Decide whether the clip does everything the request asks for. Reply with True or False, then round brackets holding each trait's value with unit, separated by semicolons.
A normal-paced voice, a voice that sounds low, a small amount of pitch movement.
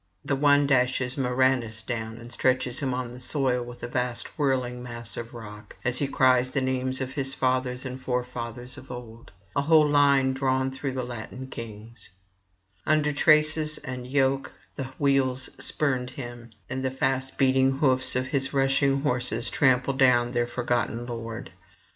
True (160 wpm; 130 Hz; 1.7 semitones)